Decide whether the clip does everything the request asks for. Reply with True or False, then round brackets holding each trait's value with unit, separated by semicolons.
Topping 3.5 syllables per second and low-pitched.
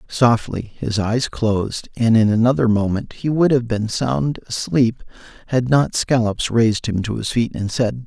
True (4.4 syllables/s; 115 Hz)